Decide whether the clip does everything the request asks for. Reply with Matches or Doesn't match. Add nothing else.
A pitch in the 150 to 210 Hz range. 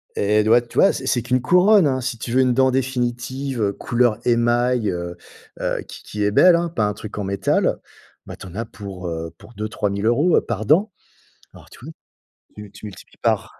Doesn't match